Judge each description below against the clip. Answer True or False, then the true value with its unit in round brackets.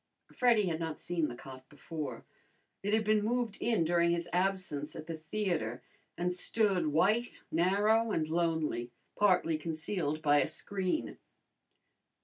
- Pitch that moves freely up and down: False (4.7 semitones)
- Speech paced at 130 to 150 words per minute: True (140 wpm)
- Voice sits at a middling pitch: True (175 Hz)